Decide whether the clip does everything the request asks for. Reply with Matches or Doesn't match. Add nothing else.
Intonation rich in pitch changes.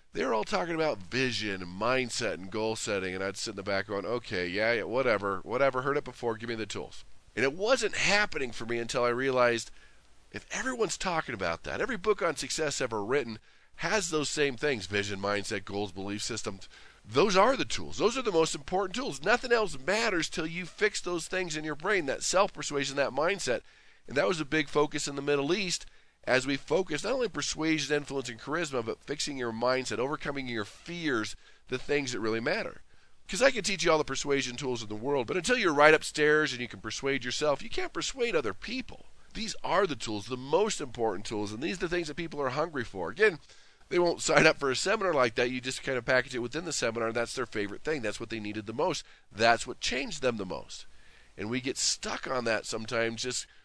Matches